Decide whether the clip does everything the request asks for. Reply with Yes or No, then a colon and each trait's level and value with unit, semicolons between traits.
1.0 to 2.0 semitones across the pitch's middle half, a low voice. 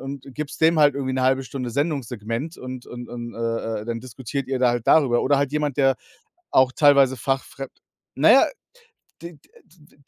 No: average, 2.8 semitones; low, 130 Hz